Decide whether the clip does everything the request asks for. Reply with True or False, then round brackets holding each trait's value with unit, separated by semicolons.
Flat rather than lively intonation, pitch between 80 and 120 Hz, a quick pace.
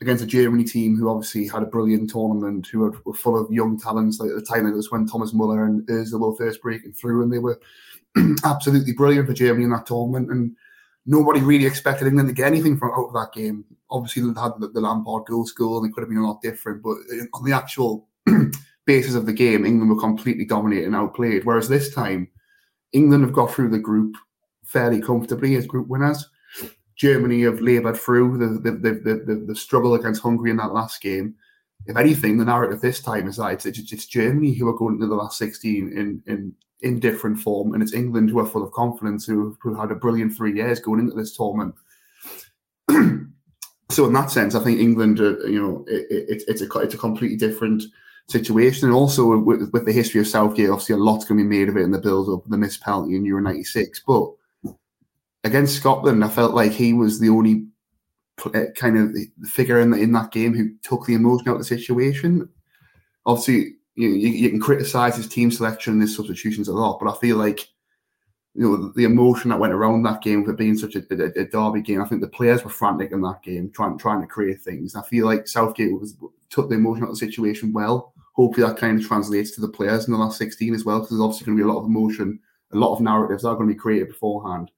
True (2.1 semitones; 110 Hz; 230 wpm)